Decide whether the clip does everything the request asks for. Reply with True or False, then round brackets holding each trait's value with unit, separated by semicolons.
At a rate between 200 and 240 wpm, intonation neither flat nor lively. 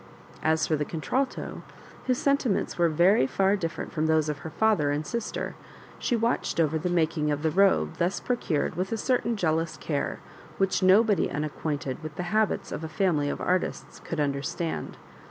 False (175 wpm; 4.5 semitones)